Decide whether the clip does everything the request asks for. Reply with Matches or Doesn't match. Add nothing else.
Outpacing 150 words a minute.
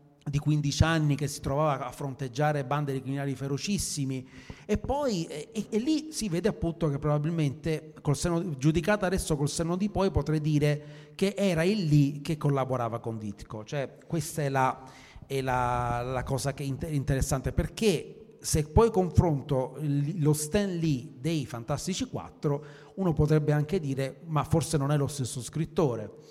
Matches